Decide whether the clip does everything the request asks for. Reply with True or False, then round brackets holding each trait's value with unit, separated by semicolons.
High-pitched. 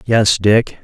False (110 Hz)